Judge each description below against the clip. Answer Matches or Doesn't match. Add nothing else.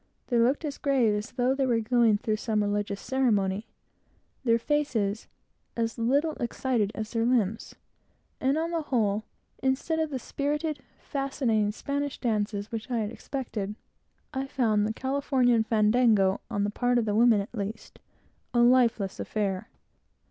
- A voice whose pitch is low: Doesn't match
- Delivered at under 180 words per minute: Matches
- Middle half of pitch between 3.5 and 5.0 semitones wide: Matches